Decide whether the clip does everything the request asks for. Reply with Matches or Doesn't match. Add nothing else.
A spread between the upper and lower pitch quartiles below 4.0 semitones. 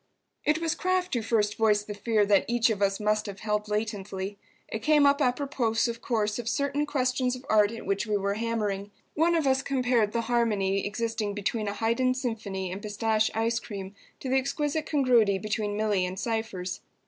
Matches